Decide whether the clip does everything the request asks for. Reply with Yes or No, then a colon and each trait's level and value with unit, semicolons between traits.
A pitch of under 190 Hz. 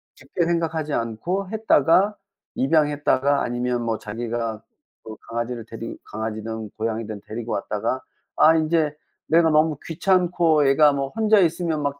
Yes: medium, 140 Hz